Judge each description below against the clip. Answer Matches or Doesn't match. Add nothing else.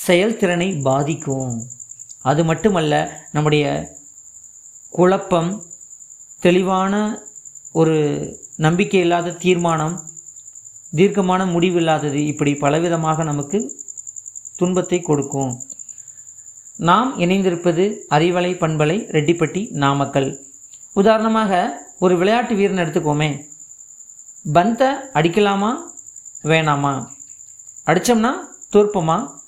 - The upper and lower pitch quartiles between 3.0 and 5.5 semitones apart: Matches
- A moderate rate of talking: Doesn't match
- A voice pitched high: Doesn't match